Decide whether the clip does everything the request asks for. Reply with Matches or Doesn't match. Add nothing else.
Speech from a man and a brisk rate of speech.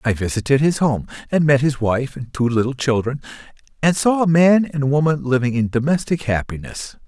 Doesn't match